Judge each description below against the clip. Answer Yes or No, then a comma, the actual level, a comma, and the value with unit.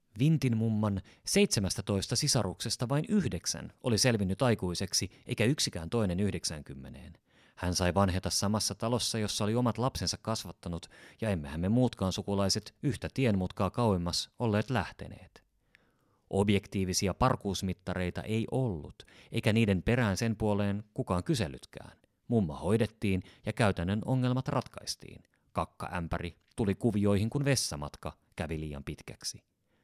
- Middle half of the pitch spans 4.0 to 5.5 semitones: Yes, average, 4.4 semitones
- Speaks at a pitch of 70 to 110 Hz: Yes, low, 105 Hz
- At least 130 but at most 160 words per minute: No, average, 120 wpm